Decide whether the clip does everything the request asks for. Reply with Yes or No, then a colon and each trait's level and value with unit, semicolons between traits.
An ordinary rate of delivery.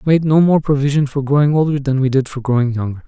No: fast, 275 wpm